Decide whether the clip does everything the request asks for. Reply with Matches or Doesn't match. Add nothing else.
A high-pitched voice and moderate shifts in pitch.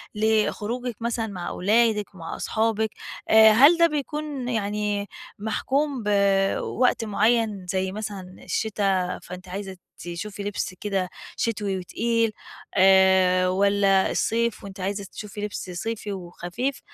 Matches